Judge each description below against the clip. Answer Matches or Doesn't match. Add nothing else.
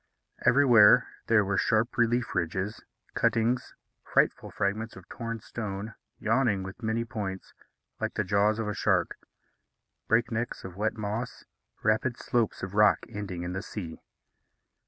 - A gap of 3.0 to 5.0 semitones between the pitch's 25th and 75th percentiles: Doesn't match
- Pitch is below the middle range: Matches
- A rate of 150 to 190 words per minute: Doesn't match